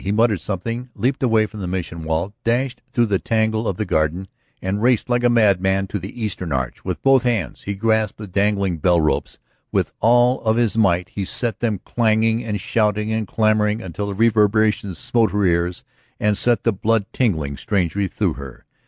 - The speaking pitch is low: Yes, low, 105 Hz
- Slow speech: No, average, 195 wpm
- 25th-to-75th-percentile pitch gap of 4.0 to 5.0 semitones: No, average, 3.3 semitones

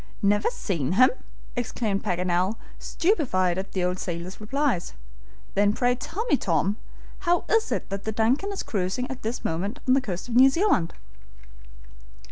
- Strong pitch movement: Yes, wide, 6.1 semitones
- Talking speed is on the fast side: No, average, 160 wpm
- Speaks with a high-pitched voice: Yes, high, 215 Hz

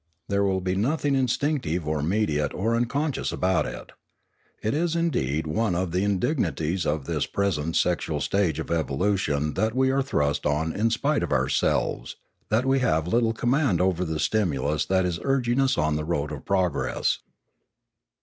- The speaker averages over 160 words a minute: Yes, average, 170 wpm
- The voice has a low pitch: Yes, very low, 95 Hz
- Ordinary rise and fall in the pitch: No, wide, 7.4 semitones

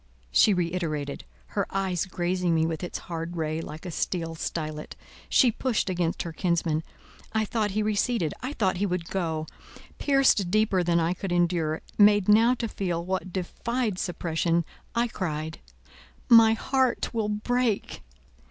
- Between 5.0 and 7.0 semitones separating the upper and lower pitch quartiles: No, average, 4.3 semitones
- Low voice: No, medium, 180 Hz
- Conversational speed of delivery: Yes, average, 150 wpm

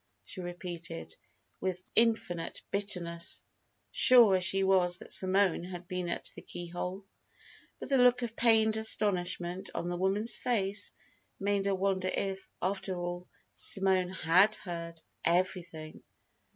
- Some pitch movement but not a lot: No, narrow, 2.2 semitones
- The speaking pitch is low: No, medium, 185 Hz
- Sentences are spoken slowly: Yes, slow, 130 wpm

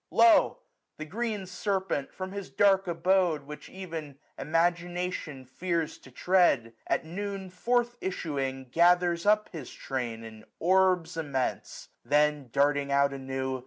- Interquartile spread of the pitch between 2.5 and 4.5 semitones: No, average, 5.2 semitones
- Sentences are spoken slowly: Yes, slow, 130 wpm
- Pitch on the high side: No, medium, 165 Hz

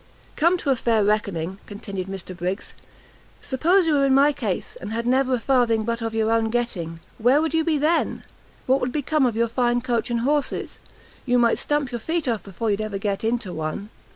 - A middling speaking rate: No, fast, 210 wpm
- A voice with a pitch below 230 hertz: No, high, 235 Hz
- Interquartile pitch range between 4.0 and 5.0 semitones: Yes, average, 4.5 semitones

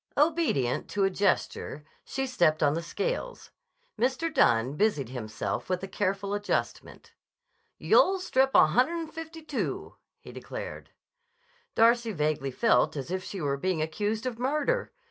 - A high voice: Yes, high, 205 Hz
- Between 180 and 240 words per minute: No, average, 145 wpm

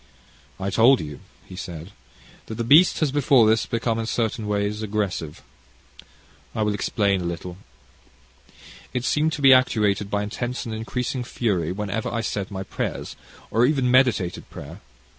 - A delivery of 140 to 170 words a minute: Yes, average, 160 wpm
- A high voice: No, low, 110 Hz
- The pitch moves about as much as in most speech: Yes, average, 3.9 semitones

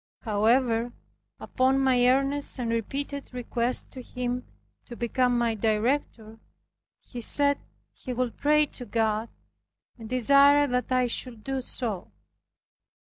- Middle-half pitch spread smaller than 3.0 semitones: Yes, narrow, 2.6 semitones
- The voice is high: Yes, very high, 250 Hz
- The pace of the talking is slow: Yes, slow, 125 wpm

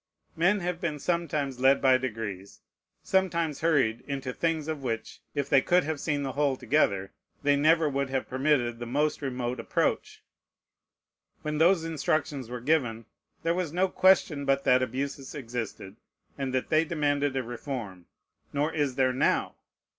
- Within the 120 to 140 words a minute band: No, average, 160 wpm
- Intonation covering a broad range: No, average, 3.6 semitones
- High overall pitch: No, medium, 140 Hz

